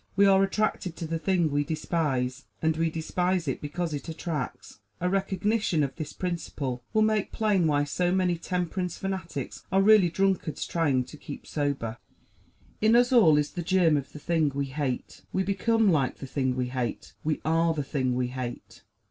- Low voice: No, medium, 165 Hz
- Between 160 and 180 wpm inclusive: No, average, 190 wpm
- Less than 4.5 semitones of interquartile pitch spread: No, average, 4.8 semitones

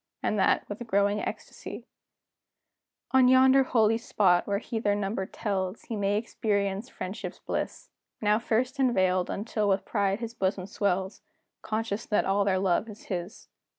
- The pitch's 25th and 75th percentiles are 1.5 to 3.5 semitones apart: Yes, narrow, 2.6 semitones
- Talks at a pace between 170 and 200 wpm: No, average, 150 wpm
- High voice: Yes, high, 205 Hz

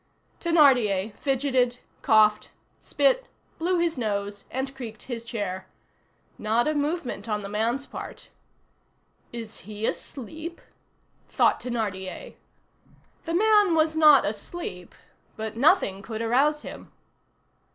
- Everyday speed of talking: No, slow, 110 wpm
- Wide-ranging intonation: Yes, wide, 6.4 semitones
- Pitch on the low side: No, high, 245 Hz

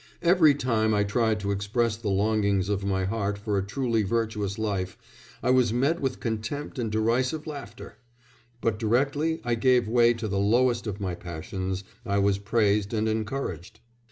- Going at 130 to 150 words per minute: No, average, 170 wpm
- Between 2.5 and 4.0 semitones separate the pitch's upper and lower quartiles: Yes, average, 3.3 semitones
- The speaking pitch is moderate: No, low, 110 Hz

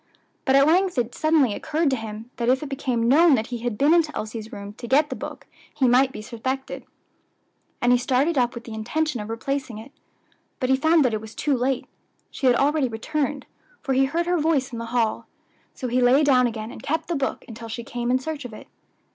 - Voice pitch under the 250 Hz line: No, very high, 260 Hz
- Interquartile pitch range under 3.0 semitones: No, average, 3.8 semitones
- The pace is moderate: No, fast, 230 wpm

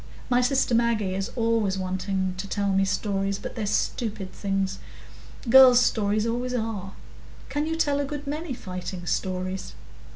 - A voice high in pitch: Yes, high, 210 Hz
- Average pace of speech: Yes, average, 155 wpm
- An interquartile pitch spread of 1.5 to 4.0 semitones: No, average, 4.4 semitones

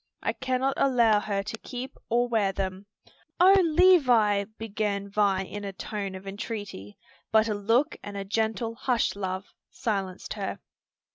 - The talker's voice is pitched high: Yes, high, 210 Hz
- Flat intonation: No, average, 3.3 semitones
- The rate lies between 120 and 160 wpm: Yes, average, 150 wpm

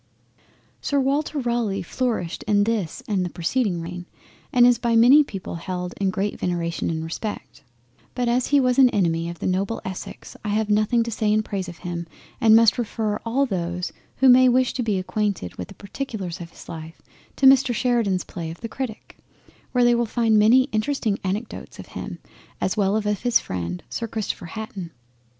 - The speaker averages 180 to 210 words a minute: Yes, average, 190 wpm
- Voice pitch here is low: No, high, 210 Hz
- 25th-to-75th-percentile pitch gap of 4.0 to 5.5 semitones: Yes, average, 5.2 semitones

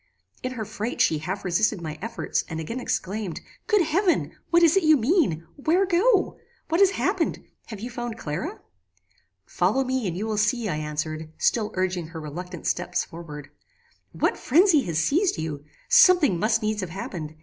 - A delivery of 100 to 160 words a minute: No, average, 175 wpm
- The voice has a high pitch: Yes, high, 215 Hz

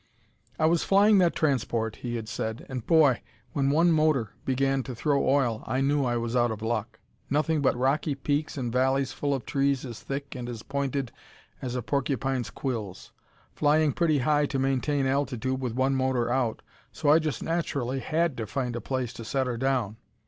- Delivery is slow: No, average, 190 wpm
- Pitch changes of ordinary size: Yes, average, 3.0 semitones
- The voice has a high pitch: No, low, 135 Hz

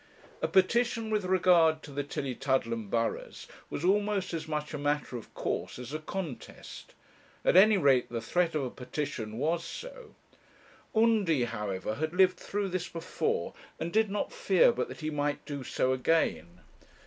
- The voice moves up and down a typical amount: No, wide, 6.6 semitones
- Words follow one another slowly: No, average, 165 wpm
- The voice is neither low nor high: Yes, medium, 155 Hz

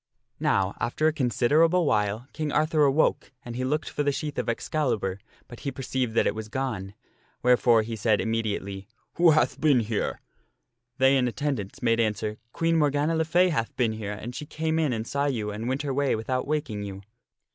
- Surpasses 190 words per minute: Yes, average, 200 wpm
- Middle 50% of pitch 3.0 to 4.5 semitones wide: No, average, 5.2 semitones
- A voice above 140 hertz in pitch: No, low, 125 Hz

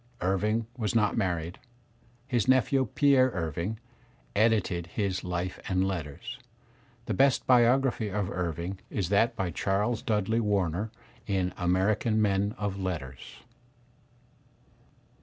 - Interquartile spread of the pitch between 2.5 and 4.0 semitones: Yes, average, 3.7 semitones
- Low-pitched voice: Yes, low, 100 Hz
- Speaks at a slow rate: Yes, slow, 115 wpm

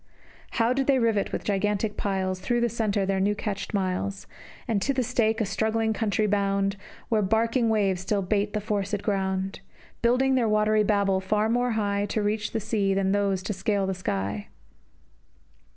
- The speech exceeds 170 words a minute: Yes, average, 180 wpm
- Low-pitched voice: No, high, 205 Hz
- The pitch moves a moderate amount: No, narrow, 2.2 semitones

